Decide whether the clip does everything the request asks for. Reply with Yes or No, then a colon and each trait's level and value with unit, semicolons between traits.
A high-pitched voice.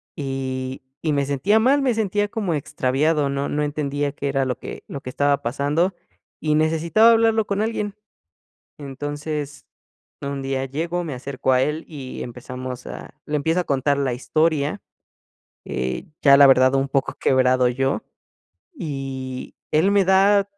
No: medium, 145 Hz